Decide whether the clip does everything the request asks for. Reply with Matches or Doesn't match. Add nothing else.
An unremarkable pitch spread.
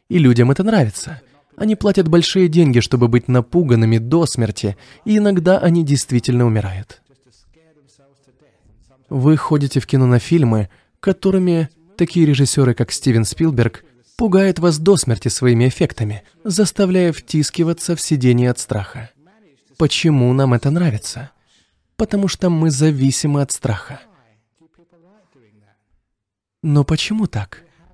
Doesn't match